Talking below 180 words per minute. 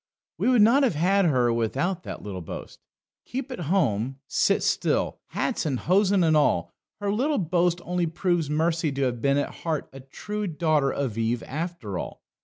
No: average, 185 wpm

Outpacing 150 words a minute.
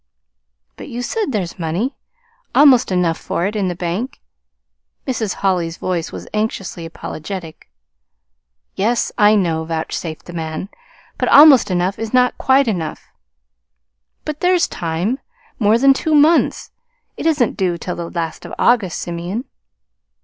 No: average, 140 wpm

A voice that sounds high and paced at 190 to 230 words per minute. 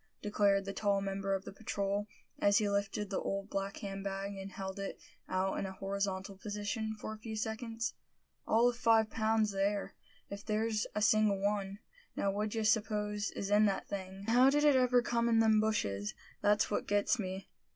Yes: high, 205 Hz; average, 195 wpm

